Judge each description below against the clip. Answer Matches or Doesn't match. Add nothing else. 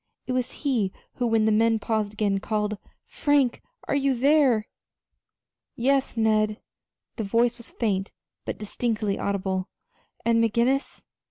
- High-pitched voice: Matches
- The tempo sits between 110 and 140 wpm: Matches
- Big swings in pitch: Doesn't match